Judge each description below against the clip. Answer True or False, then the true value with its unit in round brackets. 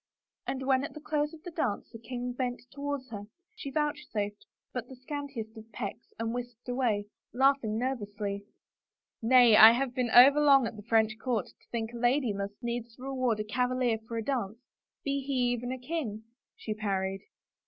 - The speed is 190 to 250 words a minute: True (195 wpm)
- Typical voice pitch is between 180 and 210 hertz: False (245 Hz)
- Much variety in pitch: False (3.4 semitones)